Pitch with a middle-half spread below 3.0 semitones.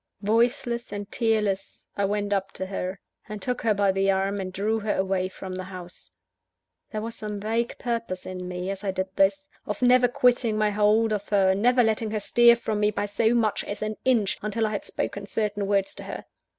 Yes: narrow, 2.5 semitones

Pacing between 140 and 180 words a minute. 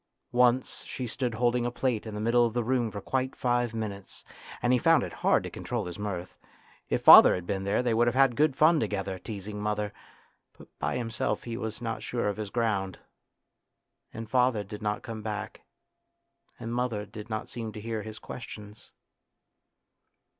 No: average, 190 wpm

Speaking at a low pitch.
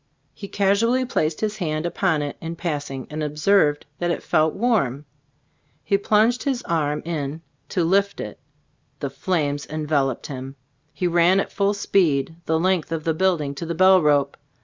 No: medium, 165 Hz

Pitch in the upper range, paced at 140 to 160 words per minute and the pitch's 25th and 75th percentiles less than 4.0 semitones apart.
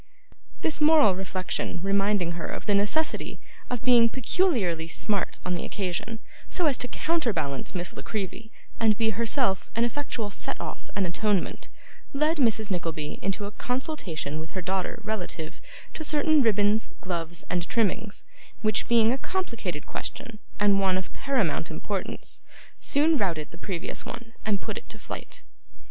No: high, 205 Hz; average, 155 wpm; average, 4.8 semitones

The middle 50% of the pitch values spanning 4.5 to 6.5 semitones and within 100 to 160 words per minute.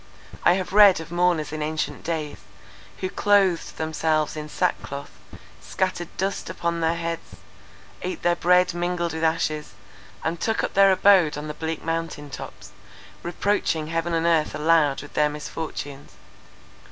No: narrow, 2.6 semitones; average, 150 wpm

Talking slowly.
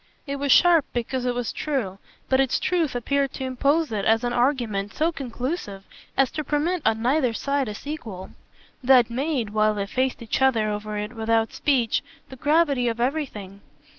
No: average, 180 wpm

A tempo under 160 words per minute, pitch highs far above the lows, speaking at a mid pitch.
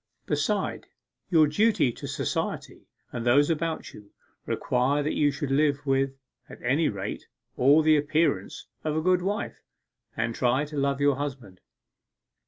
No: average, 150 wpm; average, 2.8 semitones; medium, 145 Hz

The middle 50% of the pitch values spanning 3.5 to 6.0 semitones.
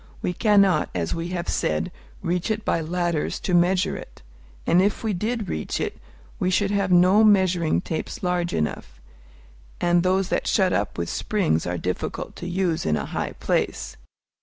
No: average, 3.0 semitones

